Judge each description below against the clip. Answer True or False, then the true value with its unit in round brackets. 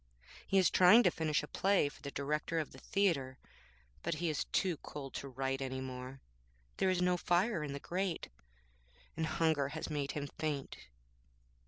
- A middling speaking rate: True (180 wpm)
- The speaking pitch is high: False (150 Hz)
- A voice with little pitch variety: False (4.2 semitones)